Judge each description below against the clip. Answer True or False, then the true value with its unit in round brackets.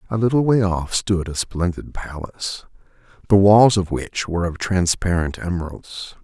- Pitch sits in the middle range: False (90 Hz)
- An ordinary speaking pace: True (155 wpm)